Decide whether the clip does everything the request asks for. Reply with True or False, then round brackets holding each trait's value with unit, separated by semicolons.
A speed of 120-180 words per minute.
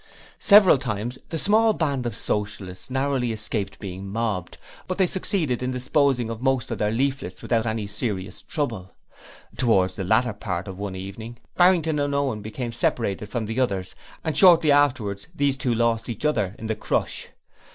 True (170 wpm)